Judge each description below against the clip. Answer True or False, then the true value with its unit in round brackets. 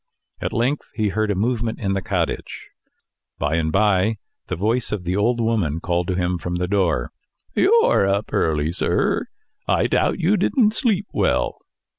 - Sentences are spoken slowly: False (170 wpm)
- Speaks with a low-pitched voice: True (100 Hz)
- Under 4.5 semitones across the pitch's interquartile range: False (4.9 semitones)